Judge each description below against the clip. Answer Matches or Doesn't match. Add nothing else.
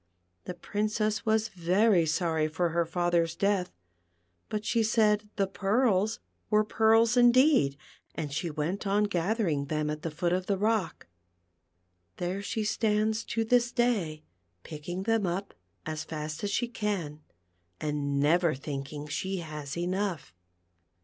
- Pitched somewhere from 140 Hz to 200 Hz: Matches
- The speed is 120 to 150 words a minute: Matches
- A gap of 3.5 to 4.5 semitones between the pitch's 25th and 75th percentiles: Doesn't match